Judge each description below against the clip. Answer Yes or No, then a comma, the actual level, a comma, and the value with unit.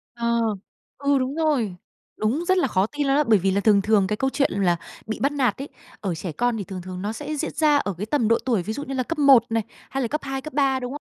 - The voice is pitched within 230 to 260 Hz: Yes, high, 245 Hz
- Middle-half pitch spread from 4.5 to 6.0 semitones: Yes, wide, 5.4 semitones